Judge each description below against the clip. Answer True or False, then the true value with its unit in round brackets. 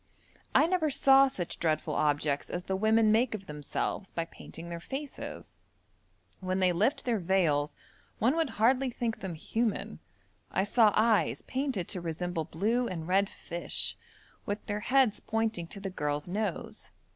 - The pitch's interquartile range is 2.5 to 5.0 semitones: False (5.4 semitones)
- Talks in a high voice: True (200 Hz)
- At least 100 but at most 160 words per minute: True (155 wpm)